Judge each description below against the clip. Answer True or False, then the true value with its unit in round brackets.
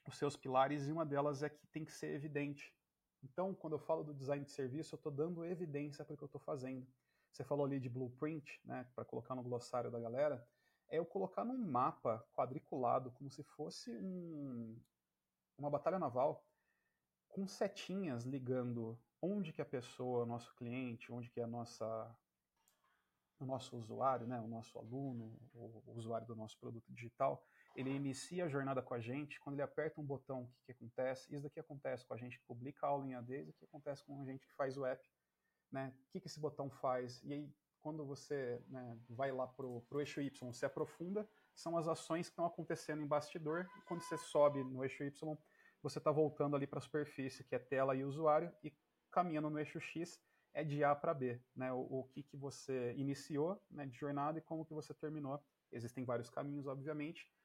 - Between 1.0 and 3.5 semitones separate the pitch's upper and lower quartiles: True (3.2 semitones)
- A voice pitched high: False (140 Hz)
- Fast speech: True (205 wpm)